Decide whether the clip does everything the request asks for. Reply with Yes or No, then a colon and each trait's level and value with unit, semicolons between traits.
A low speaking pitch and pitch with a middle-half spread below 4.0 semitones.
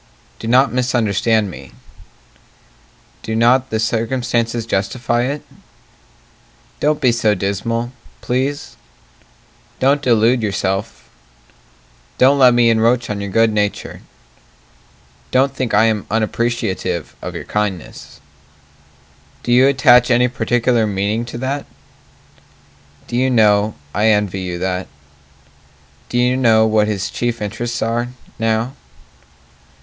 Yes: low, 115 Hz; average, 2.8 semitones